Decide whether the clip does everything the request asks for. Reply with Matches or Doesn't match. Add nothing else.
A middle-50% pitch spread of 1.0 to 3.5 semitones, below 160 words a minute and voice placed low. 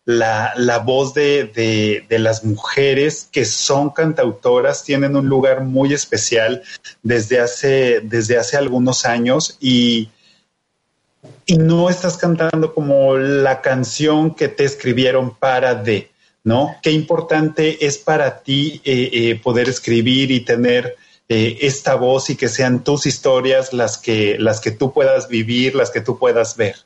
Matches